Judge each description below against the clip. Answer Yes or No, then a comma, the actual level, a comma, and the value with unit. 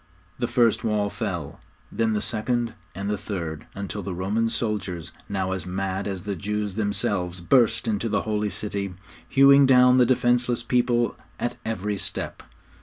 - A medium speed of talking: Yes, average, 160 wpm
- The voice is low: Yes, low, 105 Hz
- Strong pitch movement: No, average, 3.4 semitones